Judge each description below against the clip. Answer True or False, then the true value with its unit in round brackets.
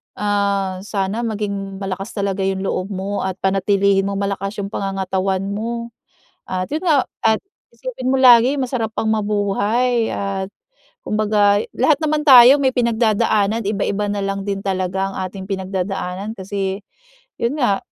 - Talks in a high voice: True (200 Hz)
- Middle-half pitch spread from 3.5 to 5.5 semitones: False (2.7 semitones)